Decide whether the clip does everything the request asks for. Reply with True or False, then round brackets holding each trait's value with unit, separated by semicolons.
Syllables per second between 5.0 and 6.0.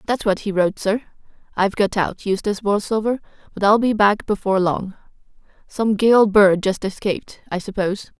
True (5.5 syllables/s)